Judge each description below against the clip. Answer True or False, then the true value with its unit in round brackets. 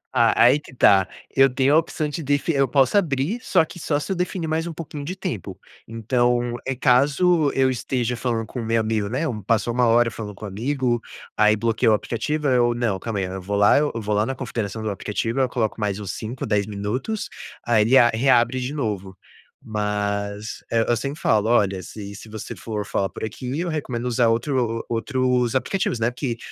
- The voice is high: False (120 Hz)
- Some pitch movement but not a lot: True (4.0 semitones)